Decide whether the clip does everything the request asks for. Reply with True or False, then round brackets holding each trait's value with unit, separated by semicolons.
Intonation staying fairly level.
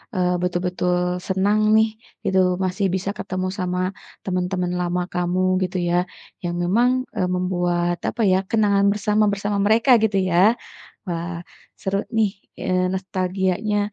True (2.1 semitones)